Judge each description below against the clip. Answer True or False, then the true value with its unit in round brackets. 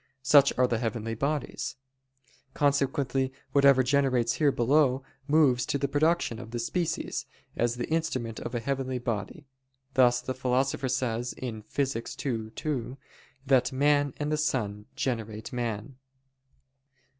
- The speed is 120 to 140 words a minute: True (135 wpm)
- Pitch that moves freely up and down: False (3.0 semitones)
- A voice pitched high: False (130 Hz)